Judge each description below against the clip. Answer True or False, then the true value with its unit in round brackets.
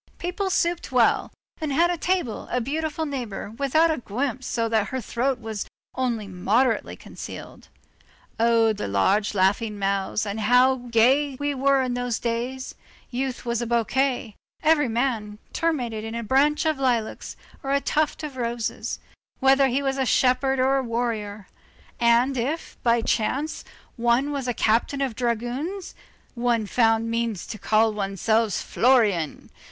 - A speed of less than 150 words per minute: False (155 wpm)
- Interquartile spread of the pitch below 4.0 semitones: True (3.4 semitones)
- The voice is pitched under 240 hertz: False (245 Hz)